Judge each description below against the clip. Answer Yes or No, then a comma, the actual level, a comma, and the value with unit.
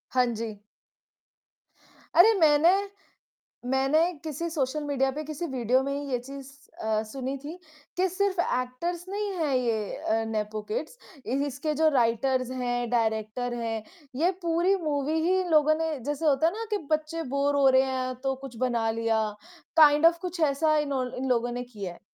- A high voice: Yes, very high, 275 Hz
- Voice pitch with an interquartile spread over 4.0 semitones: Yes, average, 4.4 semitones